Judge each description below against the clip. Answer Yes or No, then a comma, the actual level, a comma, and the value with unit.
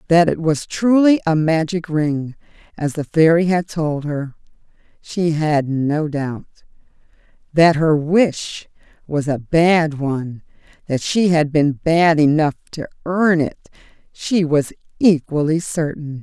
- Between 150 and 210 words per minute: No, slow, 135 wpm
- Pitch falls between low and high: Yes, medium, 160 Hz